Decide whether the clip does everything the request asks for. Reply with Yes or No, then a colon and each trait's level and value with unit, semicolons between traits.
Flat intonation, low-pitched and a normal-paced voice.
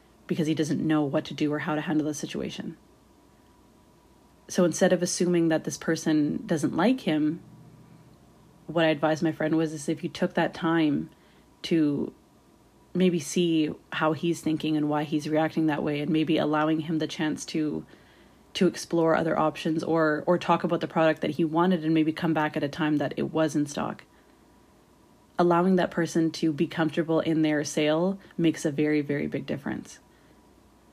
No: narrow, 1.6 semitones; medium, 160 Hz; average, 180 wpm